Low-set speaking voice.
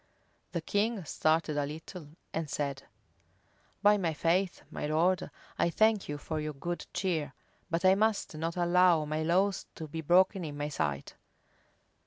No: medium, 165 Hz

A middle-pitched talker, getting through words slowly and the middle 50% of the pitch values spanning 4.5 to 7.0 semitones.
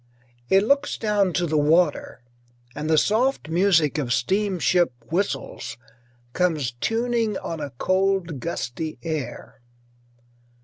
Yes: medium, 175 Hz; slow, 115 wpm; average, 5.0 semitones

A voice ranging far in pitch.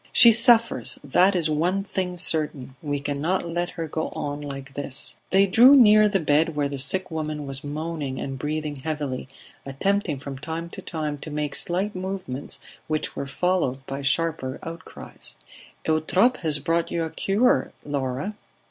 No: average, 4.4 semitones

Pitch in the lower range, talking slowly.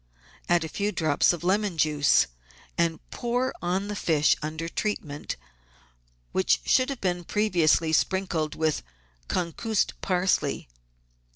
No: medium, 175 Hz; slow, 120 wpm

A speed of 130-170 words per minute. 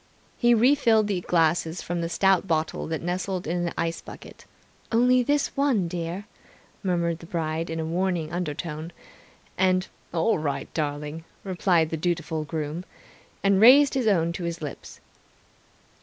Yes: average, 150 wpm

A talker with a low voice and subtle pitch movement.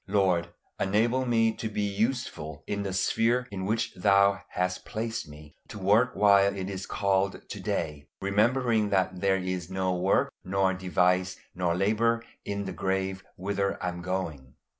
Yes: very low, 95 Hz; narrow, 2.2 semitones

